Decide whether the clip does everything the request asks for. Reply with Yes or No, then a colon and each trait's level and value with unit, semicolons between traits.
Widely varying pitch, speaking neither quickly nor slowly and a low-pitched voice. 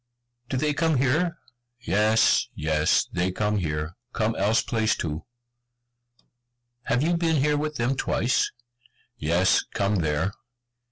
No: wide, 8.3 semitones; slow, 125 wpm; low, 110 Hz